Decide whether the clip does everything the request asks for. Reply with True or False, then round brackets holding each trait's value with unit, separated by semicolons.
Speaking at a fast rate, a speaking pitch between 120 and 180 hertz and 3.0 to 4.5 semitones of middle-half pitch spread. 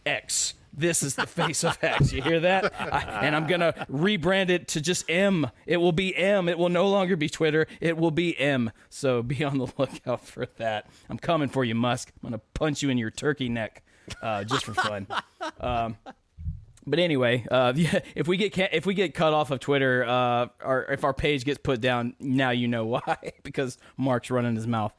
False (210 wpm; 140 Hz; 5.3 semitones)